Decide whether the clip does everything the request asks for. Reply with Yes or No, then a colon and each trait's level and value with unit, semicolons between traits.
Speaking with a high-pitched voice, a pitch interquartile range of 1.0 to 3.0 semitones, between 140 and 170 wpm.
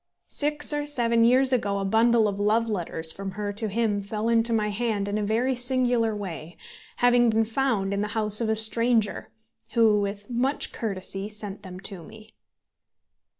No: high, 220 Hz; narrow, 2.6 semitones; average, 180 wpm